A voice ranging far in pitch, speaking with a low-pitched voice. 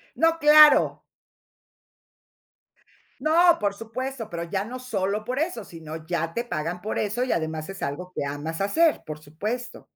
No: wide, 7.5 semitones; high, 205 Hz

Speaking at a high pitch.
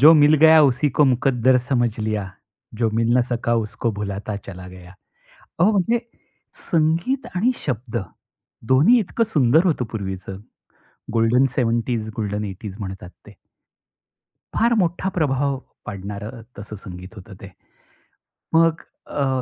No: low, 120 Hz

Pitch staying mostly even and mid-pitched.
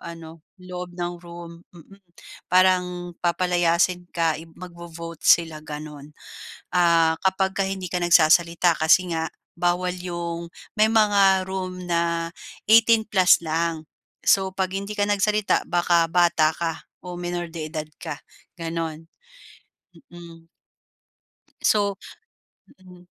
Yes: narrow, 1.7 semitones; medium, 175 Hz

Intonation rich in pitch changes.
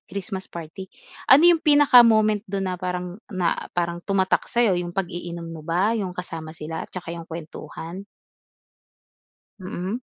No: average, 3.3 semitones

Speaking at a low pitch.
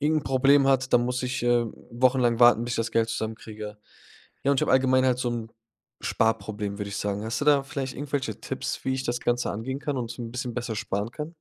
Yes: low, 120 Hz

